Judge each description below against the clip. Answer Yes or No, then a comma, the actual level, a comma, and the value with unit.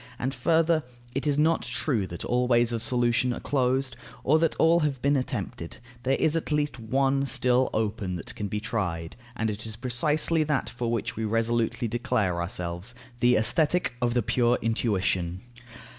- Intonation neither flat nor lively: Yes, average, 3.9 semitones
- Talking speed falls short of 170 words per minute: No, average, 175 wpm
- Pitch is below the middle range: Yes, low, 120 Hz